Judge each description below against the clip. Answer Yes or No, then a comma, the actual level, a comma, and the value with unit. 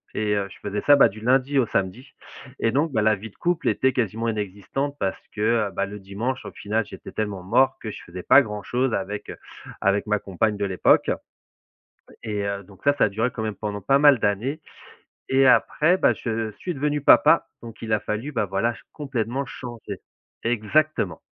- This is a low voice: Yes, low, 110 Hz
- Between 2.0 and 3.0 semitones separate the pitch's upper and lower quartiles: No, average, 4.5 semitones